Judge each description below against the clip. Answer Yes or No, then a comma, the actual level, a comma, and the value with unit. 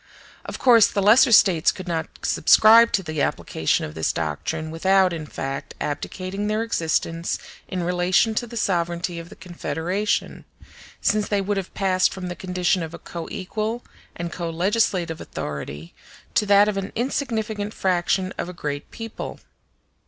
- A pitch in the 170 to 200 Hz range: Yes, medium, 185 Hz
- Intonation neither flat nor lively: Yes, average, 3.9 semitones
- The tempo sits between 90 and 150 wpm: No, average, 160 wpm